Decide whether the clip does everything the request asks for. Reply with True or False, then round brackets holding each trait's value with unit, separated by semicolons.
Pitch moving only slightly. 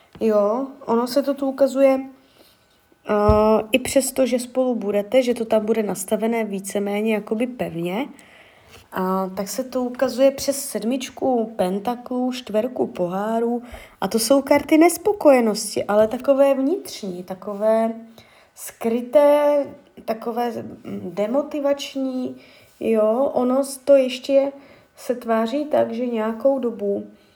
False (4.2 semitones)